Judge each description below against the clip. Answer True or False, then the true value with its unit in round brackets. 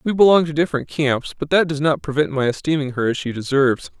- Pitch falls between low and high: True (145 Hz)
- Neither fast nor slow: False (240 wpm)